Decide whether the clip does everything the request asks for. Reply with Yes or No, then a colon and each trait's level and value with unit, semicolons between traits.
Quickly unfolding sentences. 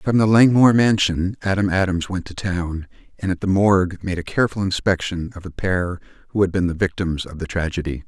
Yes: fast, 210 wpm